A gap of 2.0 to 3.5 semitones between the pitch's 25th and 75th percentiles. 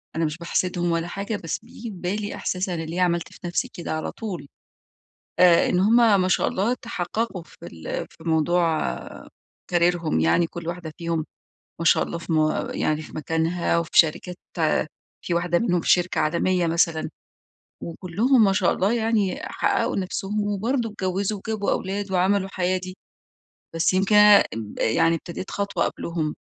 Yes: average, 3.1 semitones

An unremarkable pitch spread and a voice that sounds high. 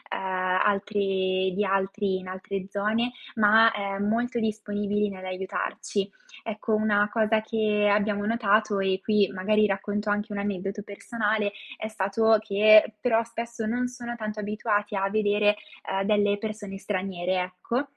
No: narrow, 1.7 semitones; high, 205 Hz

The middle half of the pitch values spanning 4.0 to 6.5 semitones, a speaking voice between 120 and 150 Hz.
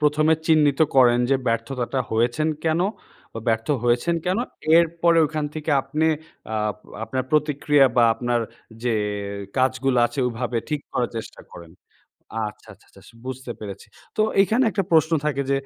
Yes: average, 4.5 semitones; low, 135 Hz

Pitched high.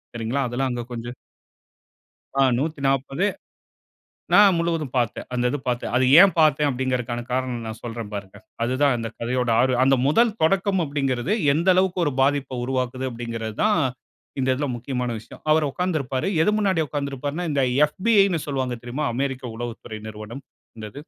No: low, 130 Hz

